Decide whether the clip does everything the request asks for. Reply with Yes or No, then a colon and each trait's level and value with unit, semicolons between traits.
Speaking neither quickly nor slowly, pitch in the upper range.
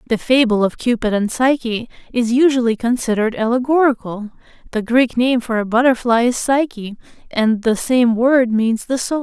Yes: average, 165 wpm; high, 240 Hz